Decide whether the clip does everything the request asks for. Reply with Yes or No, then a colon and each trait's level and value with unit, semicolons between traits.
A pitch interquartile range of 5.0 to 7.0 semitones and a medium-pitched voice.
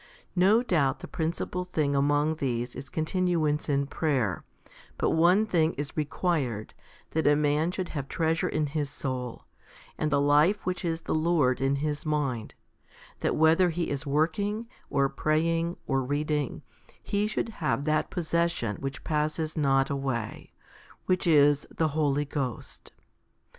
No: average, 3.1 semitones; medium, 150 Hz